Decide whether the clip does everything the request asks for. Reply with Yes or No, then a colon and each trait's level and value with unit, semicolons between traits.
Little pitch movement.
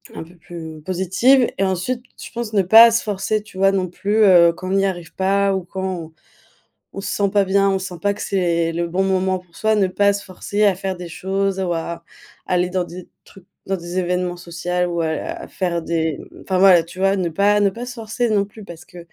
Yes: narrow, 2.3 semitones